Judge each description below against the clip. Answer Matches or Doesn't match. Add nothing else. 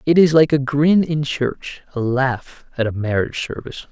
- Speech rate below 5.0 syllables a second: Matches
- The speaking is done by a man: Matches